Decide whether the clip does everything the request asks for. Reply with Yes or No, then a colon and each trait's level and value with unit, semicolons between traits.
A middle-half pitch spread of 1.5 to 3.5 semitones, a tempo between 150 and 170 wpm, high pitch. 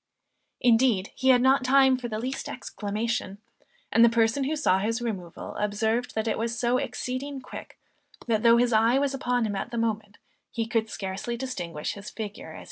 No: average, 2.7 semitones; average, 200 wpm; high, 230 Hz